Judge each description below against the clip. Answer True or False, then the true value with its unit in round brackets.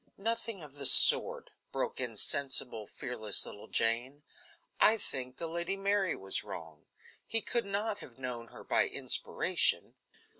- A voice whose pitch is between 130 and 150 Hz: True (135 Hz)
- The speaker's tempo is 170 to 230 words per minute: False (145 wpm)